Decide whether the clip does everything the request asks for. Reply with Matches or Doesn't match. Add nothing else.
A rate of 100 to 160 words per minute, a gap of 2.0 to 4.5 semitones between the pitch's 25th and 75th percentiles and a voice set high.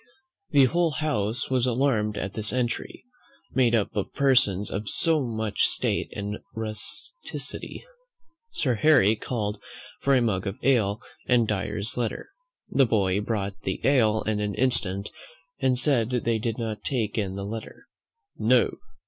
Doesn't match